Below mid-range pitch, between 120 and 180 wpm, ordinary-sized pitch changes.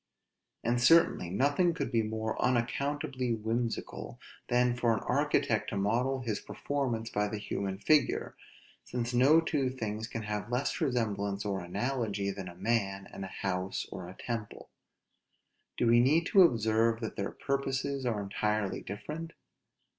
Yes: low, 115 Hz; average, 145 wpm; average, 4.2 semitones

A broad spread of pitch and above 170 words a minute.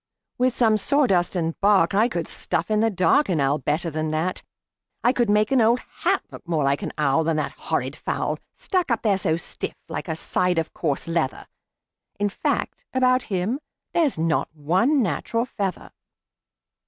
Yes: wide, 6.3 semitones; average, 180 wpm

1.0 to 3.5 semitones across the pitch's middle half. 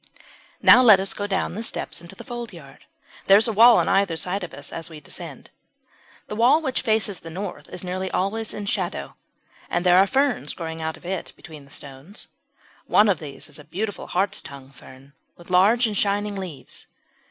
No: average, 4.6 semitones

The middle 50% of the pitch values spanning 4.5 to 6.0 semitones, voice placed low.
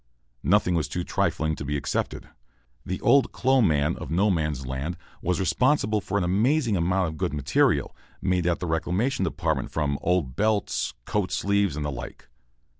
Yes: average, 4.9 semitones; very low, 90 Hz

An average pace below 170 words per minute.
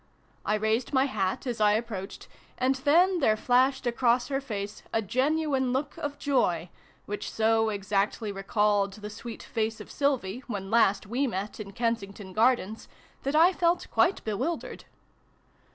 Yes: average, 150 wpm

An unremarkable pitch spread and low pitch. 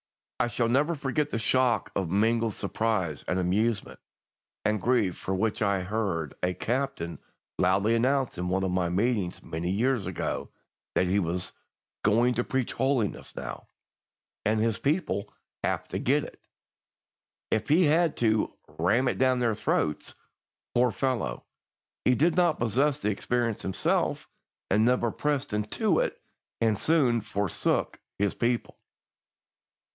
Yes: average, 4.8 semitones; low, 115 Hz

